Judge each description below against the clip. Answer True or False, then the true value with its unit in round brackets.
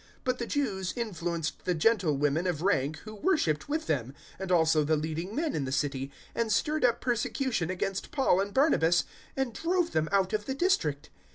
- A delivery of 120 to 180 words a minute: False (190 wpm)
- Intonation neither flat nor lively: False (7.8 semitones)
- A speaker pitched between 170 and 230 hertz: True (190 Hz)